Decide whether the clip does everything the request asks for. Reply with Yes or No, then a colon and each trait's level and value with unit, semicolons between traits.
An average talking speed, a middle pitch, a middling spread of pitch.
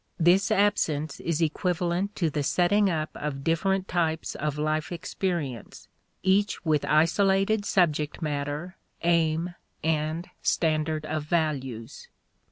No: slow, 115 wpm; medium, 160 Hz; average, 3.0 semitones